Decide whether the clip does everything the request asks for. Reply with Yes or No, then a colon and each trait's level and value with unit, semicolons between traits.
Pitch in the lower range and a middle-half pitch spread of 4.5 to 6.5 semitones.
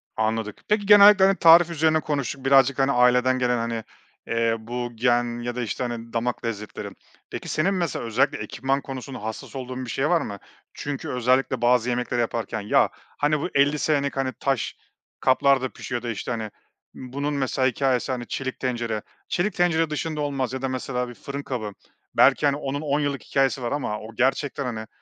No: low, 130 Hz; average, 3.0 semitones